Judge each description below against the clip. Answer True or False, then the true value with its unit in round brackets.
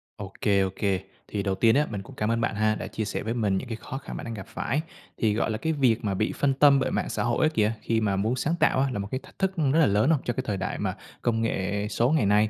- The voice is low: True (115 Hz)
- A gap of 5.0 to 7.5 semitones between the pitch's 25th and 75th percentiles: False (4.3 semitones)